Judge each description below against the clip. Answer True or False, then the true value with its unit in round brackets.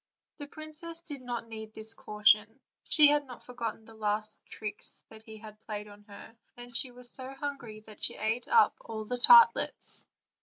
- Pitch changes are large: False (4.0 semitones)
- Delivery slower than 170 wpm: False (185 wpm)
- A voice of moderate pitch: False (230 Hz)